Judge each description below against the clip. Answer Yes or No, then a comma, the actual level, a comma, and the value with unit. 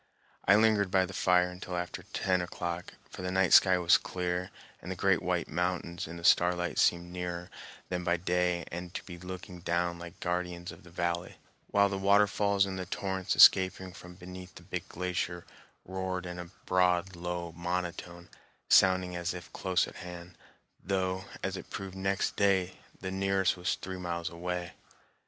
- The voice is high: No, very low, 90 Hz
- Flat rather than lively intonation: Yes, narrow, 1.2 semitones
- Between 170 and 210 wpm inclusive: Yes, average, 175 wpm